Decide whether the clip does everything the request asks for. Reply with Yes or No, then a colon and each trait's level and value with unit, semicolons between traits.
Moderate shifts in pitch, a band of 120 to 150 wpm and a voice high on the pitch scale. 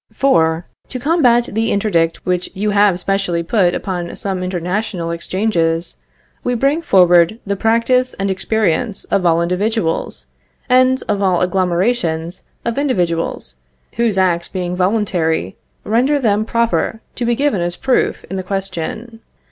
Yes: average, 4.7 semitones; average, 140 wpm; high, 195 Hz